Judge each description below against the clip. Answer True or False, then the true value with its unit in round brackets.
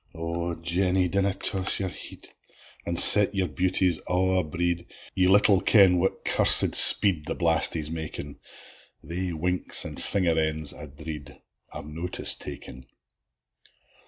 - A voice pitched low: True (85 Hz)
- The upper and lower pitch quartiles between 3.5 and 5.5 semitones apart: False (2.8 semitones)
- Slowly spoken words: True (130 wpm)